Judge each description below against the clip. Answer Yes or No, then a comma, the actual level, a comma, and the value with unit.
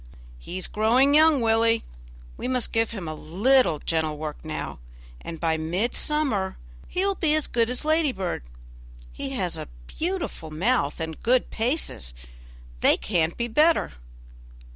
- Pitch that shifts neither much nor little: No, wide, 8.8 semitones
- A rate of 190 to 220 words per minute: No, average, 145 wpm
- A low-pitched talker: No, high, 225 Hz